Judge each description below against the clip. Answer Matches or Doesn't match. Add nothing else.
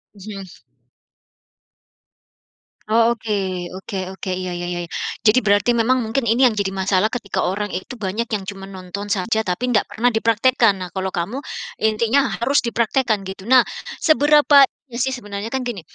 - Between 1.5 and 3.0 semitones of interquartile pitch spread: Doesn't match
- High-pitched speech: Matches